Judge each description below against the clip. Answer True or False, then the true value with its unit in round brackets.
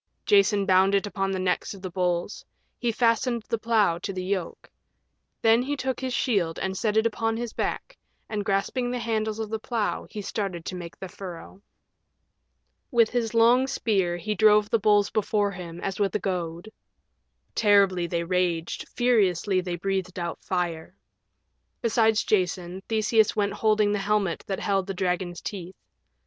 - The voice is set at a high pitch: True (200 Hz)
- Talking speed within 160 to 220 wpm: True (170 wpm)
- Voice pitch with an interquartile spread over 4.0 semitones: False (3.3 semitones)